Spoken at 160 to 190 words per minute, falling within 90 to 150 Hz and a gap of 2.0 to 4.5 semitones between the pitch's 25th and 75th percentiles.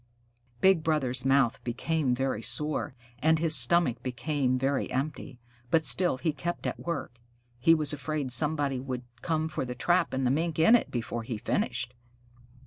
Yes: average, 165 wpm; medium, 140 Hz; average, 4.1 semitones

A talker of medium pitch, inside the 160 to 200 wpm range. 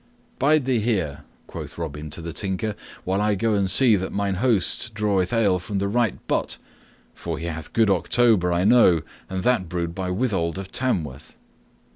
No: very low, 95 Hz; average, 180 wpm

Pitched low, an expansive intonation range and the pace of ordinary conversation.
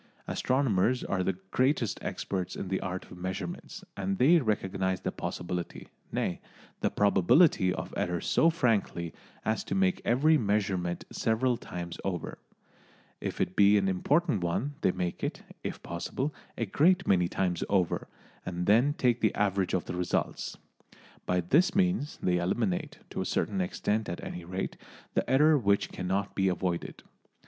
Yes: low, 100 Hz; wide, 5.8 semitones; average, 155 wpm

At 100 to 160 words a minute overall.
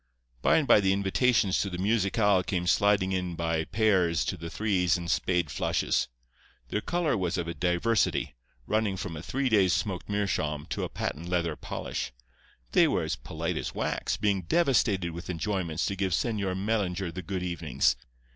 No: average, 175 wpm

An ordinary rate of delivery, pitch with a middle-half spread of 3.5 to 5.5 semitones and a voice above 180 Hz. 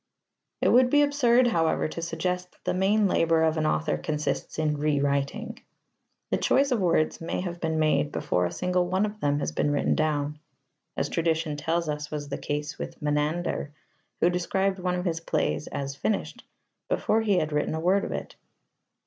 No: average, 190 wpm; average, 3.8 semitones; medium, 165 Hz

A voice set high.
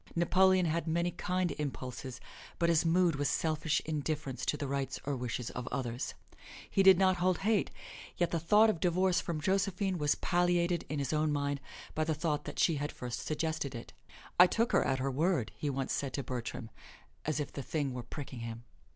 No: medium, 155 Hz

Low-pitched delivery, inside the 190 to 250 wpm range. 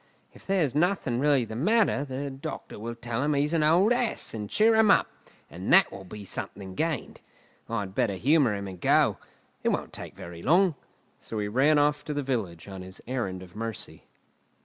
Yes: low, 130 Hz; average, 195 wpm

